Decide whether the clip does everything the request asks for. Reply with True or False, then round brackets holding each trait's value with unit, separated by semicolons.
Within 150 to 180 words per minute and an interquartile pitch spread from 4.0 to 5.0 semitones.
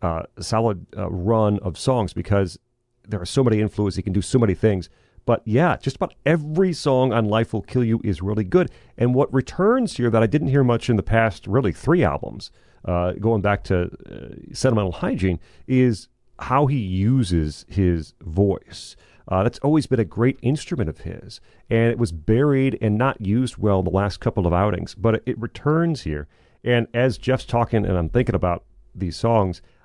False (195 wpm; 4.7 semitones)